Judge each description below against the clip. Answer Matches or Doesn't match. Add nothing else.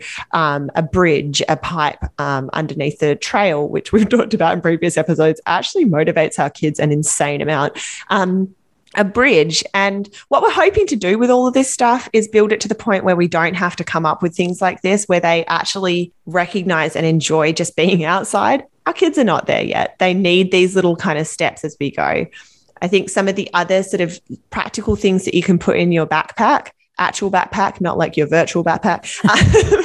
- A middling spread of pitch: Matches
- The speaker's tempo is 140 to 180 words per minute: Doesn't match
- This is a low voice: Doesn't match